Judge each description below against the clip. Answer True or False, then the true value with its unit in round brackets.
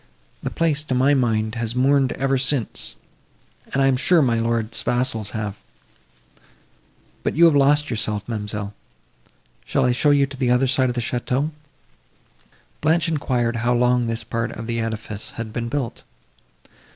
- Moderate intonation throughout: True (3.2 semitones)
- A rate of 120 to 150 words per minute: False (160 wpm)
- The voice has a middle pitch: False (125 Hz)